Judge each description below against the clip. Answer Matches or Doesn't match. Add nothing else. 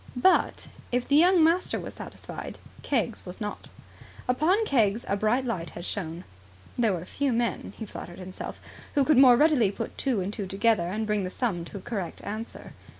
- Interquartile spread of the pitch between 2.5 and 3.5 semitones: Doesn't match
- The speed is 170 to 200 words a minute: Matches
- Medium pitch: Doesn't match